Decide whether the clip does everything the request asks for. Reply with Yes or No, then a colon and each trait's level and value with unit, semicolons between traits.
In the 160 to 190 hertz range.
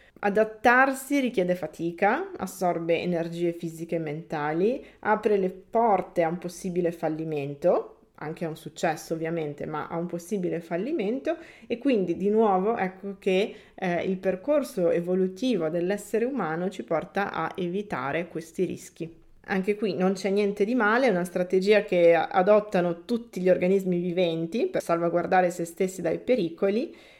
Yes: medium, 185 Hz